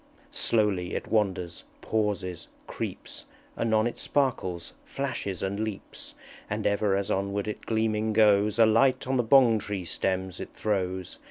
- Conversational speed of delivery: Yes, average, 145 wpm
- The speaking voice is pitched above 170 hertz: No, low, 105 Hz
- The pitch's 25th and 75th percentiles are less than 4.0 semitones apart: Yes, average, 2.7 semitones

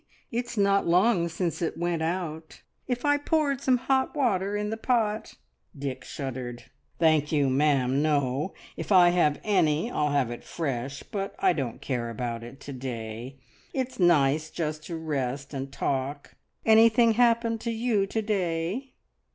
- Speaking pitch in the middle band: Yes, medium, 165 Hz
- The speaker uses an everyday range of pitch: No, wide, 8.0 semitones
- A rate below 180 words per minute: Yes, average, 160 wpm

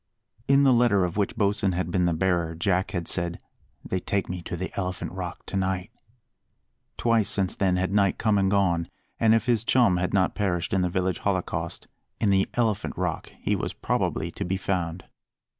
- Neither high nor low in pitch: No, very low, 95 Hz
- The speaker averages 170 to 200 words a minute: Yes, average, 195 wpm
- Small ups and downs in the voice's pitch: Yes, narrow, 2.3 semitones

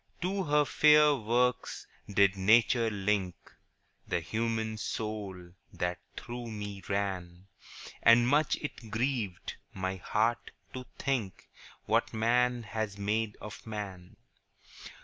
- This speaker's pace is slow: Yes, slow, 110 wpm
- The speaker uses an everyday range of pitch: Yes, average, 3.6 semitones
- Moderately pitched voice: No, low, 110 Hz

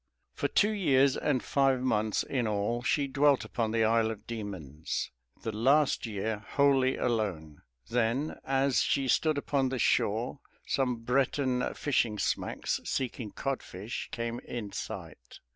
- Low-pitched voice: Yes, low, 120 Hz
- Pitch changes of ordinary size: Yes, average, 3.8 semitones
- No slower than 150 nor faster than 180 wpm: No, average, 140 wpm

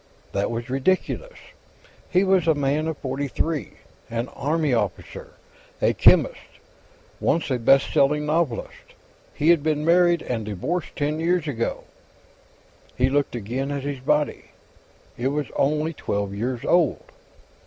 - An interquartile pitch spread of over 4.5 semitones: No, average, 4.1 semitones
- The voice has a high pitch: No, medium, 145 Hz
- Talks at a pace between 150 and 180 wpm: No, average, 140 wpm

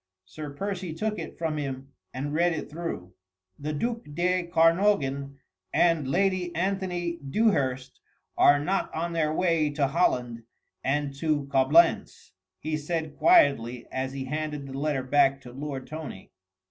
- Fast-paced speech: No, average, 145 wpm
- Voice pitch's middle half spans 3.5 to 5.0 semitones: Yes, average, 3.9 semitones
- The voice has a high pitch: No, medium, 150 Hz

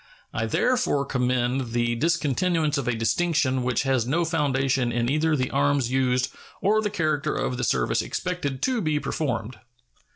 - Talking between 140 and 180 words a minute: Yes, average, 160 wpm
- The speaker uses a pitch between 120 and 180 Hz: Yes, low, 135 Hz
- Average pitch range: Yes, average, 4.2 semitones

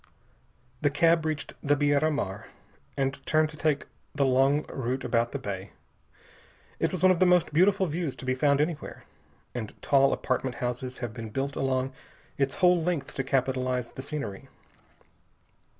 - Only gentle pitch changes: No, average, 3.3 semitones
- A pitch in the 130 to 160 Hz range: Yes, medium, 140 Hz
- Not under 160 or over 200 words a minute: Yes, average, 165 wpm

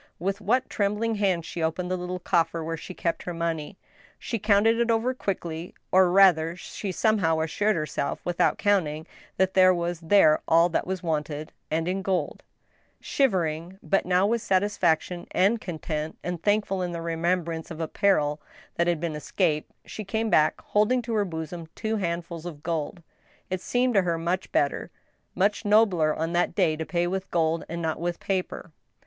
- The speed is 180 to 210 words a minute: Yes, average, 185 wpm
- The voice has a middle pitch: Yes, medium, 175 Hz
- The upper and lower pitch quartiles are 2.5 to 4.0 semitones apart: Yes, average, 3.4 semitones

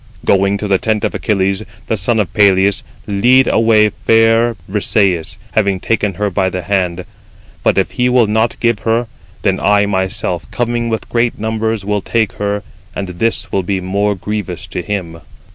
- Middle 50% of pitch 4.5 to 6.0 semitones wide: No, average, 2.7 semitones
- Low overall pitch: Yes, low, 105 Hz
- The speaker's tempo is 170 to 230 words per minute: Yes, average, 180 wpm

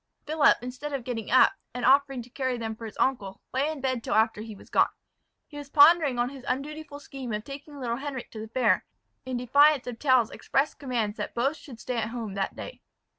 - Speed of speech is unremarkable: No, fast, 225 wpm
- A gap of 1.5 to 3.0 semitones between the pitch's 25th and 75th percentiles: No, average, 3.5 semitones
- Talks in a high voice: Yes, very high, 255 Hz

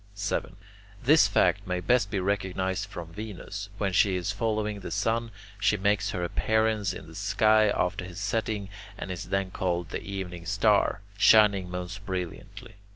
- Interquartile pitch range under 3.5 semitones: Yes, narrow, 2.4 semitones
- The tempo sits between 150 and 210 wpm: Yes, average, 160 wpm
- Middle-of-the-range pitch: No, low, 100 Hz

